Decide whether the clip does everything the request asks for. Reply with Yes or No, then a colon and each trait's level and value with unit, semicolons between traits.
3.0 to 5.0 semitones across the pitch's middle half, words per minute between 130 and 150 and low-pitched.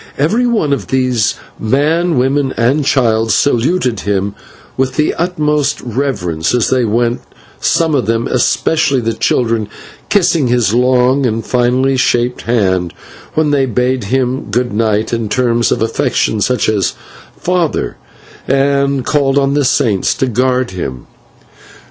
Yes: average, 3.5 semitones; average, 140 wpm; low, 125 Hz